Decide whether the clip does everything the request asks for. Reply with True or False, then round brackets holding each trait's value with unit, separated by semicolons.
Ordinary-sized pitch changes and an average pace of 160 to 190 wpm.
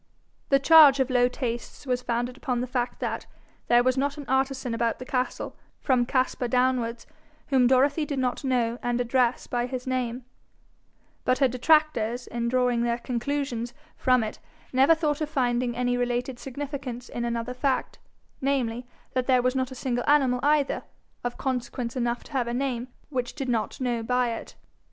False (1.7 semitones; 175 wpm)